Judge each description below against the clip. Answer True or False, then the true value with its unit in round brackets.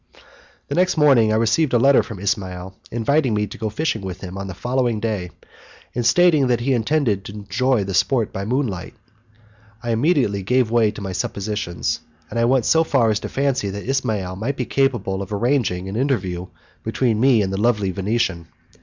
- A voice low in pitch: True (110 Hz)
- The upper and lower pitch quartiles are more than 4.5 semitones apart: True (4.9 semitones)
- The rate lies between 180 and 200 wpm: True (195 wpm)